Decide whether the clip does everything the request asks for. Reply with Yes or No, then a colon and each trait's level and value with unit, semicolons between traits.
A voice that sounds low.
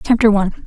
No: high, 210 Hz